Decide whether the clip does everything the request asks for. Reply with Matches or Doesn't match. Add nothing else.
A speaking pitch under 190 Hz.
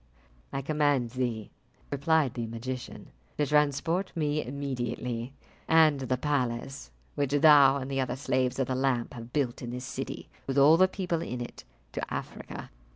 Matches